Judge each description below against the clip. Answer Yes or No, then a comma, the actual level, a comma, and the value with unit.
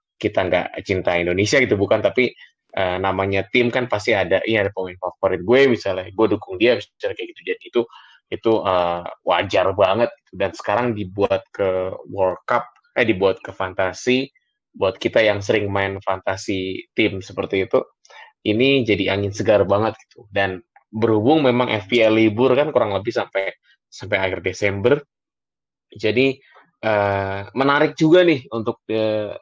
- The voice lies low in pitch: Yes, low, 110 Hz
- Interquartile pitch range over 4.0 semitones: Yes, average, 5.3 semitones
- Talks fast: Yes, fast, 150 wpm